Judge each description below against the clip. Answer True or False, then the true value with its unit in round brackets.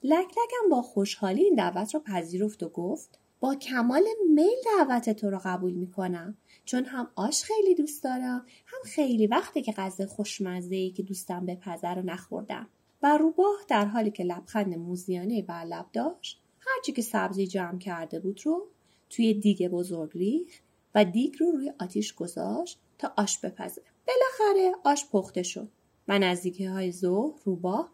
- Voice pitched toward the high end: True (215 Hz)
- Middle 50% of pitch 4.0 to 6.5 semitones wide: False (8.5 semitones)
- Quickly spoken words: True (165 wpm)